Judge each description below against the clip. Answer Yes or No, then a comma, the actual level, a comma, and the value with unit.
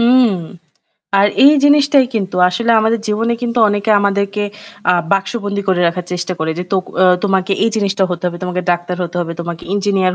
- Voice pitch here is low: No, high, 200 Hz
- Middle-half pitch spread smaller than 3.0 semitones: No, average, 3.5 semitones